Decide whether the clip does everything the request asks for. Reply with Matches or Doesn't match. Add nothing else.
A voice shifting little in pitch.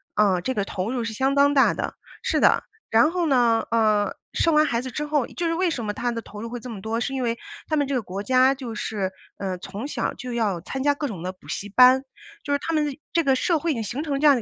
Doesn't match